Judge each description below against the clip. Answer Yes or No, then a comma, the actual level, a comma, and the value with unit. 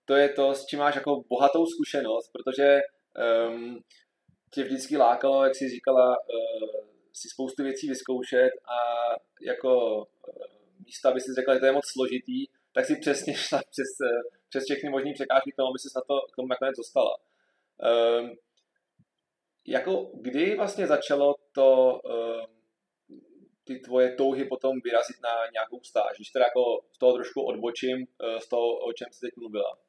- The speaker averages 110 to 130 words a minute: No, average, 165 wpm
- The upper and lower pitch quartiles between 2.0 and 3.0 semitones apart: Yes, narrow, 2.3 semitones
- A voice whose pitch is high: No, low, 135 Hz